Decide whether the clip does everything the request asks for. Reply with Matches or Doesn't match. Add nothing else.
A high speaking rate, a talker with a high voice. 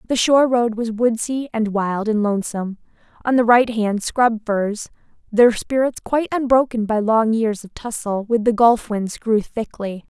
Doesn't match